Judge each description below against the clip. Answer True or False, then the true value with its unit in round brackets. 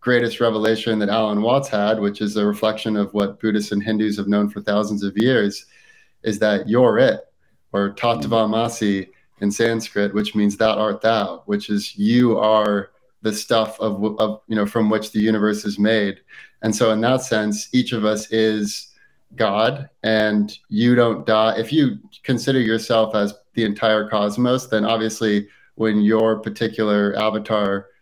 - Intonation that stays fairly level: True (1.5 semitones)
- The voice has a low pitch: True (110 Hz)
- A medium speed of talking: True (170 wpm)